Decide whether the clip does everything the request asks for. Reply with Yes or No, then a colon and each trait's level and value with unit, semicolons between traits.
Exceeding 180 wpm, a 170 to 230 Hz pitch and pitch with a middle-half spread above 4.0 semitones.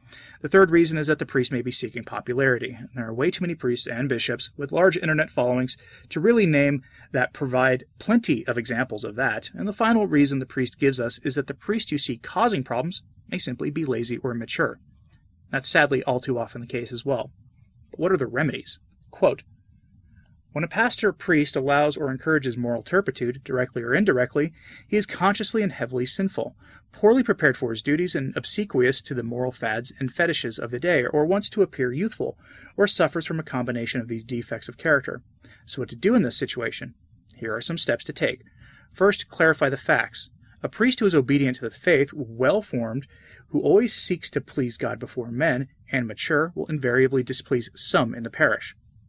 No: average, 200 wpm; low, 135 Hz; wide, 5.4 semitones